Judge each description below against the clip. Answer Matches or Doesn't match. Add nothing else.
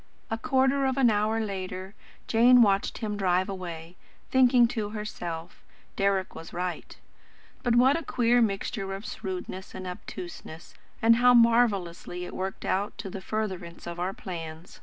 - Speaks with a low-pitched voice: Doesn't match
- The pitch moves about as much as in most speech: Matches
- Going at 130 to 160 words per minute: Matches